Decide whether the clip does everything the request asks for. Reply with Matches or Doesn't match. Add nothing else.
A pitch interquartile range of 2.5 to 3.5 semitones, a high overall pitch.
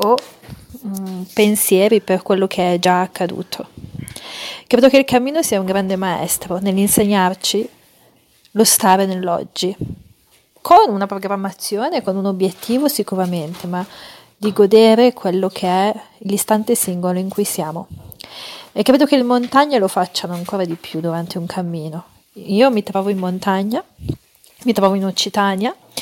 Matches